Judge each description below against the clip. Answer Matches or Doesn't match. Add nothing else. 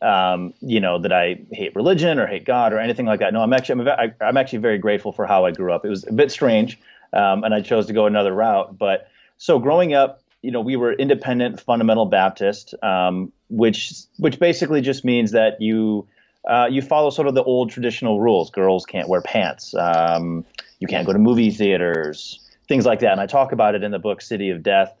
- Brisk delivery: Matches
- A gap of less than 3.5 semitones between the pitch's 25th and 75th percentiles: Doesn't match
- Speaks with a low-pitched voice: Matches